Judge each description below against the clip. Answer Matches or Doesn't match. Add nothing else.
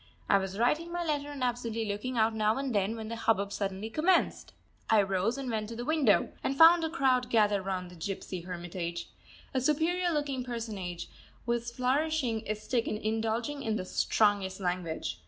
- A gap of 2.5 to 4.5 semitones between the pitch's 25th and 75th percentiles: Doesn't match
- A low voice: Doesn't match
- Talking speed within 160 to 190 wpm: Matches